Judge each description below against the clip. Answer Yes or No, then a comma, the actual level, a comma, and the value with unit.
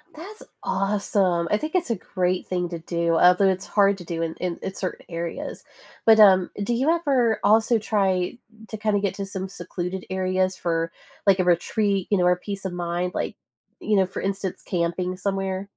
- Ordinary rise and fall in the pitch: No, narrow, 2.3 semitones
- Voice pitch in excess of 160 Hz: Yes, high, 190 Hz